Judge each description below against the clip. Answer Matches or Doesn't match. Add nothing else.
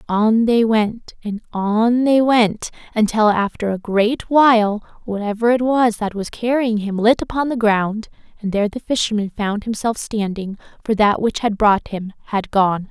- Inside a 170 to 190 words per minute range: Matches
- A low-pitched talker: Doesn't match